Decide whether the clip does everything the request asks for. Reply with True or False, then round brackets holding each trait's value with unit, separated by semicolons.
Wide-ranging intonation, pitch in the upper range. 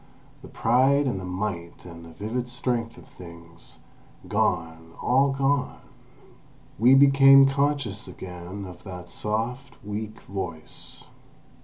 False (6.9 semitones; 105 Hz)